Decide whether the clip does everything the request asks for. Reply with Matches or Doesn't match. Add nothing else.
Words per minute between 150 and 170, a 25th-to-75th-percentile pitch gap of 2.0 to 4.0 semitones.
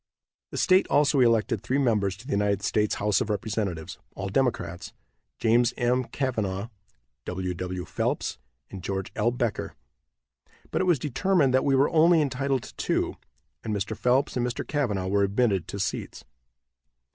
Doesn't match